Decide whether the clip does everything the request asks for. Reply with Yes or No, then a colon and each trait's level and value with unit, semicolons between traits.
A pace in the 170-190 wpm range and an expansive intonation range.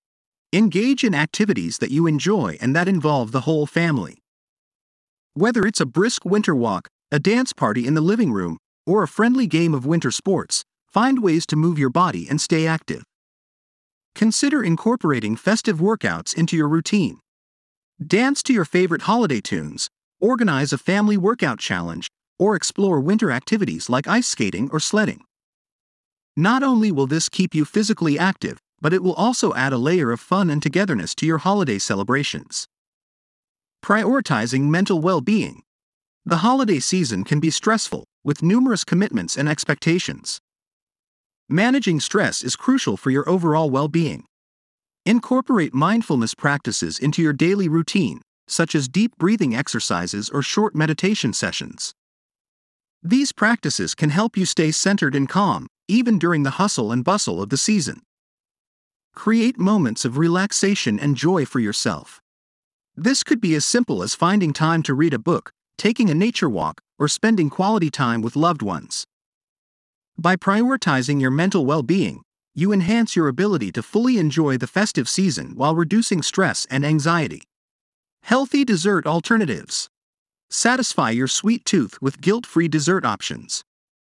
No: average, 150 wpm; wide, 6.2 semitones